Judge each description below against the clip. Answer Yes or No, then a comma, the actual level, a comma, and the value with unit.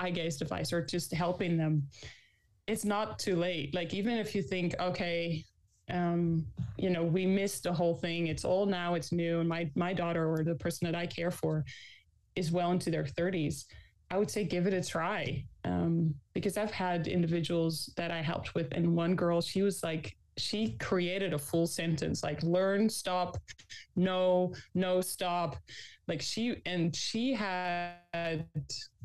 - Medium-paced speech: Yes, average, 170 wpm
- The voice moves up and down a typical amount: No, narrow, 2.0 semitones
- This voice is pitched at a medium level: Yes, medium, 175 Hz